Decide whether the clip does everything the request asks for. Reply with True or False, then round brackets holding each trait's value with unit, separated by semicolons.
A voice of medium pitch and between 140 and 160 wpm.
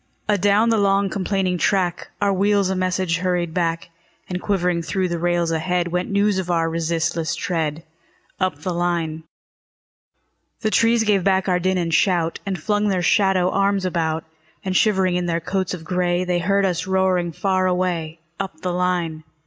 False (180 Hz; 175 wpm)